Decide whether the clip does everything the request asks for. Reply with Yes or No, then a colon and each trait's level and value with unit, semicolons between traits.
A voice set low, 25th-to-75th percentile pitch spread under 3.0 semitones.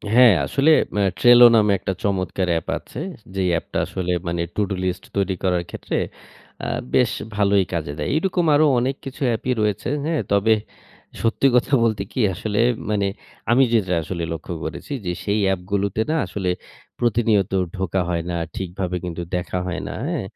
No: low, 100 Hz; average, 4.4 semitones